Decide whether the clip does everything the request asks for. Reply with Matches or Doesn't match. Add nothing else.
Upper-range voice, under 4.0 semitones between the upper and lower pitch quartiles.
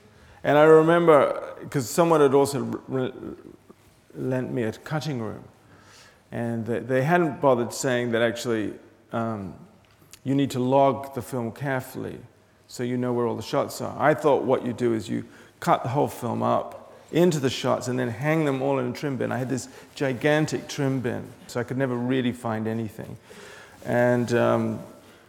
Doesn't match